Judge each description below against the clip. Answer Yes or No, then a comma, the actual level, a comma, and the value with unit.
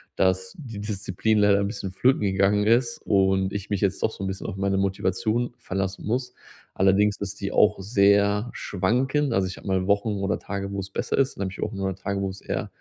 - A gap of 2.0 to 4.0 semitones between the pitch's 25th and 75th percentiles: No, narrow, 1.6 semitones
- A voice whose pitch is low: Yes, low, 100 Hz